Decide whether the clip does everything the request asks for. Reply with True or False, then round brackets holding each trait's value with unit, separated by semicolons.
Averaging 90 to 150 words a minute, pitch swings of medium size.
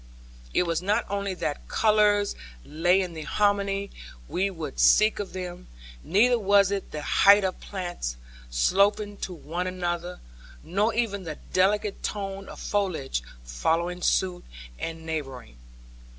True (135 wpm; 3.4 semitones)